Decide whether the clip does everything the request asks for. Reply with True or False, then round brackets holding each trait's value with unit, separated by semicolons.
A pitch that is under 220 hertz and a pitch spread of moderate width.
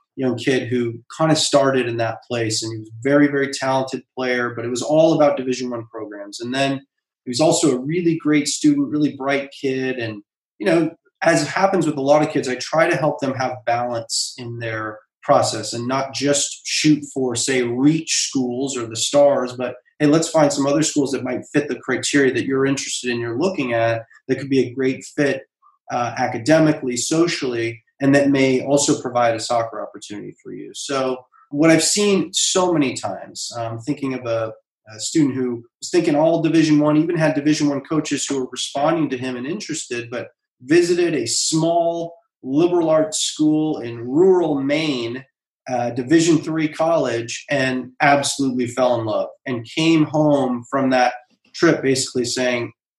True (135 Hz; 3.9 semitones)